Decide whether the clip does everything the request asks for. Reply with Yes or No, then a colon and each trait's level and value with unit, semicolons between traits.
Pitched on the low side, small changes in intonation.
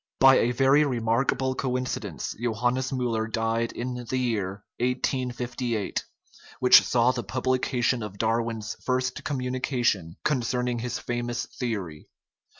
Yes: low, 125 Hz; narrow, 2.0 semitones